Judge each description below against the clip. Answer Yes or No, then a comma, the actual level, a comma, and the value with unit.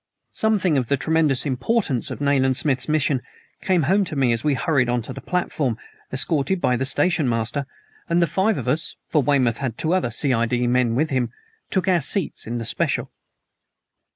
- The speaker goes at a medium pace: Yes, average, 190 wpm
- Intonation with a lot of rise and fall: No, average, 4.7 semitones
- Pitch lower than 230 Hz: Yes, medium, 140 Hz